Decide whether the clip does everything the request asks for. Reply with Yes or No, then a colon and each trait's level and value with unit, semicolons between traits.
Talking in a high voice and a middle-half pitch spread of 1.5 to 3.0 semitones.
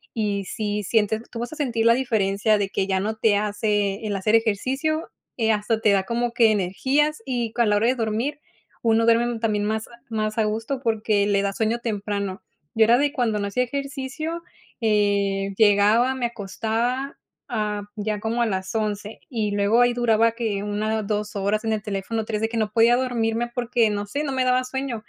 Yes: high, 220 Hz; narrow, 2.5 semitones